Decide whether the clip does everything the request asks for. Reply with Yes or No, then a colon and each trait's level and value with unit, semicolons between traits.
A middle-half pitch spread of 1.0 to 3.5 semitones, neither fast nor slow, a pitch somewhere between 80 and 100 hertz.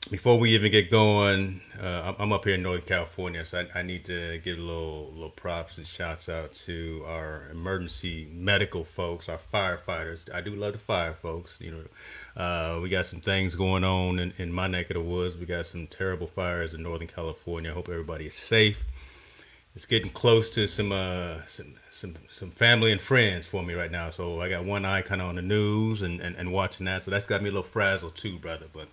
No: average, 2.8 semitones; fast, 225 wpm; very low, 90 Hz